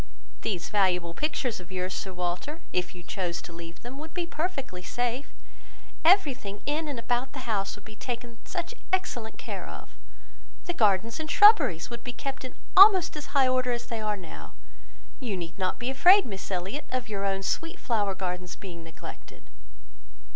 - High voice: Yes, high, 230 Hz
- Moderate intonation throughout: No, wide, 7.2 semitones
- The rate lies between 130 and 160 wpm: No, average, 180 wpm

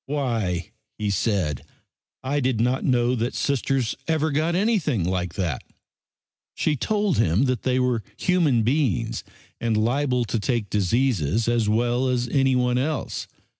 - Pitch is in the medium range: No, low, 125 Hz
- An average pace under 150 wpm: Yes, average, 140 wpm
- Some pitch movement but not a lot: Yes, average, 4.2 semitones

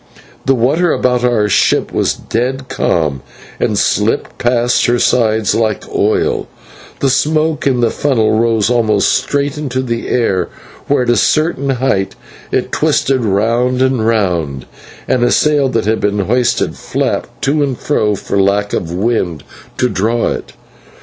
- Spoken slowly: No, average, 155 wpm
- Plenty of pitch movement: No, average, 3.8 semitones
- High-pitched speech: No, low, 120 Hz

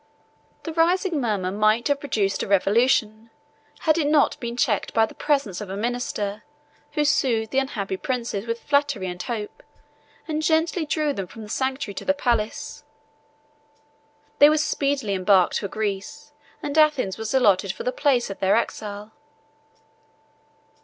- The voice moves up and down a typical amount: No, wide, 5.8 semitones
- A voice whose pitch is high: Yes, high, 235 Hz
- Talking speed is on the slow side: No, average, 155 wpm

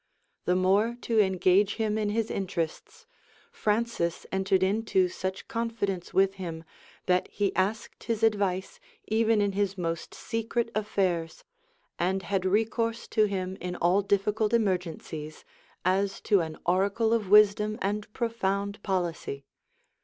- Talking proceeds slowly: Yes, slow, 130 wpm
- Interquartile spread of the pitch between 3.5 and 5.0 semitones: No, average, 2.7 semitones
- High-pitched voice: Yes, high, 200 Hz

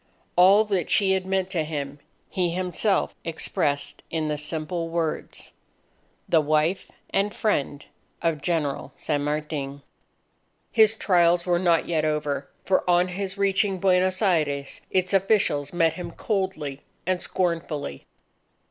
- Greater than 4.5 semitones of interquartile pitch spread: No, average, 3.8 semitones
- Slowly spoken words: Yes, slow, 130 wpm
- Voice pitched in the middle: Yes, medium, 170 Hz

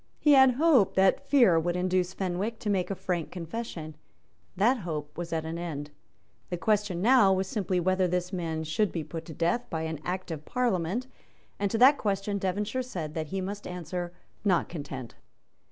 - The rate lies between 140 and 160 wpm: No, average, 185 wpm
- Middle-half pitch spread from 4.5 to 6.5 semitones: No, average, 3.9 semitones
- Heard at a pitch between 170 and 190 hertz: Yes, medium, 185 Hz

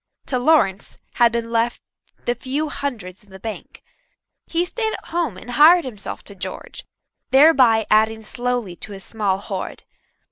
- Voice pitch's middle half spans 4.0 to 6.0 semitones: Yes, average, 5.1 semitones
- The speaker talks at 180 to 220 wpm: No, average, 155 wpm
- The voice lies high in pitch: Yes, high, 235 Hz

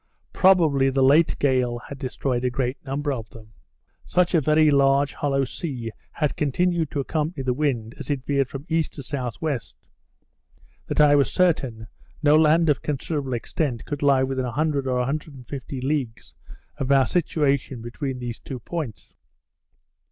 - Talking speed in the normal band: Yes, average, 160 wpm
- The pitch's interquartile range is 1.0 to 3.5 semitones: Yes, average, 2.9 semitones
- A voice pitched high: No, medium, 140 Hz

